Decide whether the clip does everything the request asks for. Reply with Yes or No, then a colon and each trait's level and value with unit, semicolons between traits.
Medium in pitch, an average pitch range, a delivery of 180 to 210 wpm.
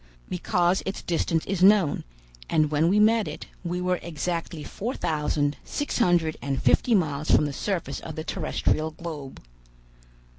No: medium, 170 Hz; average, 3.5 semitones; average, 155 wpm